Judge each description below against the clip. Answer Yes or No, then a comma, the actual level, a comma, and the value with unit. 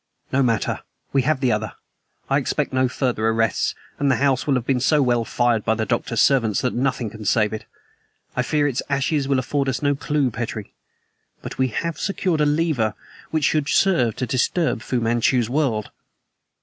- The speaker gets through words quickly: No, average, 190 wpm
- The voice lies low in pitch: Yes, low, 130 Hz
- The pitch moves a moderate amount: Yes, average, 3.8 semitones